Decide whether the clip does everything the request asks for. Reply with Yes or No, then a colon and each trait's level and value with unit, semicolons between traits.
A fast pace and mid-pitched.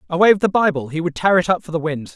Yes: fast, 335 wpm; medium, 170 Hz